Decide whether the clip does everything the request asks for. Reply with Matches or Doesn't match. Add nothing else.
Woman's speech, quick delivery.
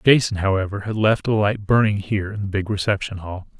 Doesn't match